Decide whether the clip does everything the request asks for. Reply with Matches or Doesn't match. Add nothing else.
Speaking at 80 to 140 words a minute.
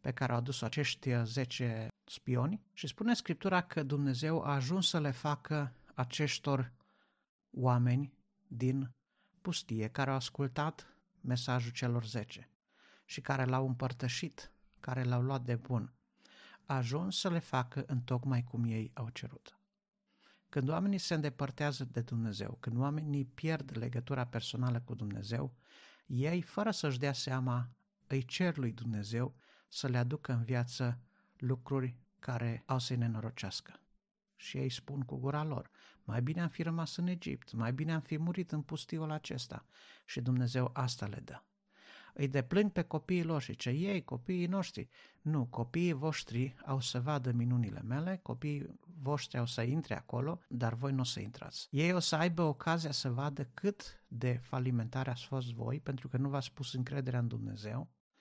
Doesn't match